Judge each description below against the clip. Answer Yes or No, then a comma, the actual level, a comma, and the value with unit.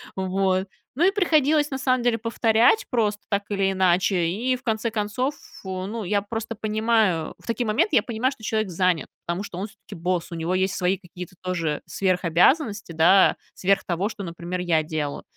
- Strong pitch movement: No, average, 4.0 semitones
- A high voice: Yes, high, 200 Hz